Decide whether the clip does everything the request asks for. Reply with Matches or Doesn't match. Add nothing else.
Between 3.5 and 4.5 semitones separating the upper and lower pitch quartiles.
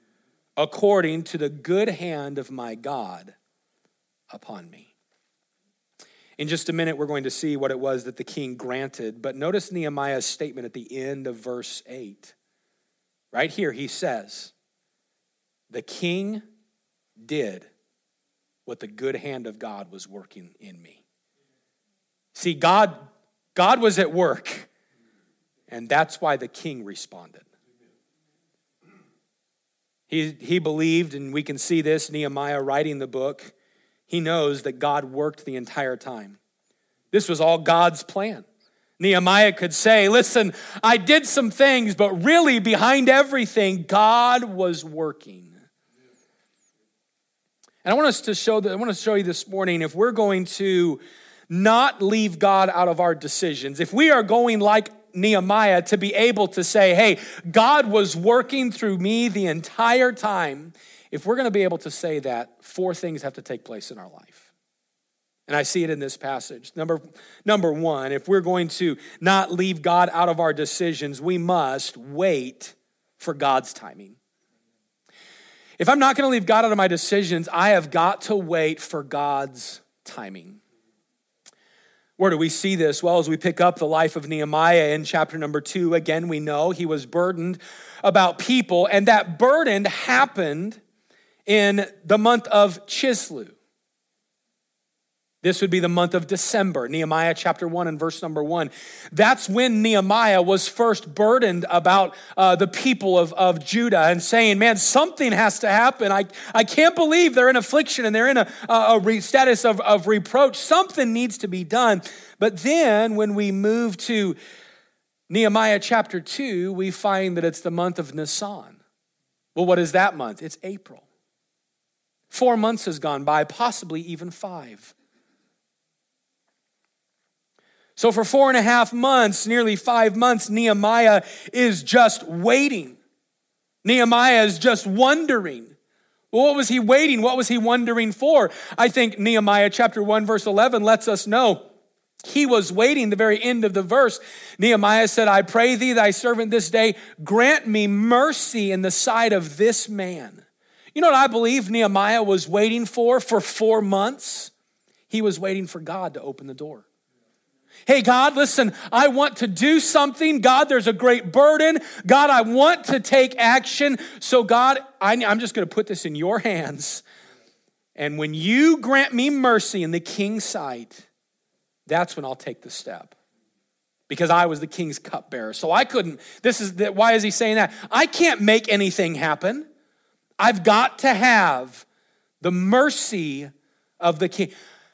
Doesn't match